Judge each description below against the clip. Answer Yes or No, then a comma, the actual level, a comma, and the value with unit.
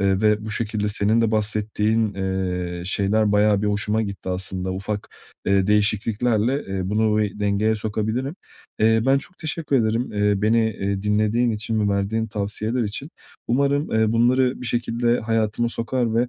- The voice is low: Yes, low, 110 Hz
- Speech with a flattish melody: Yes, narrow, 2.1 semitones